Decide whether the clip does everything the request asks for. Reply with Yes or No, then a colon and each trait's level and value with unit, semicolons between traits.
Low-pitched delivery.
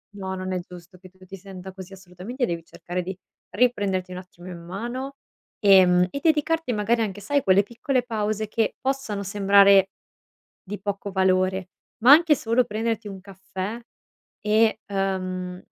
No: high, 195 Hz